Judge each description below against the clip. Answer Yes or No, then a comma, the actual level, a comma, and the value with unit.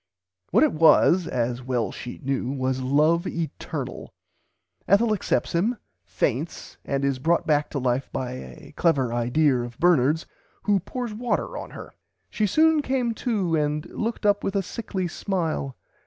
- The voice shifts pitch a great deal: Yes, wide, 7.4 semitones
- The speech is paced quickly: No, average, 155 wpm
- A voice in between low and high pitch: Yes, medium, 160 Hz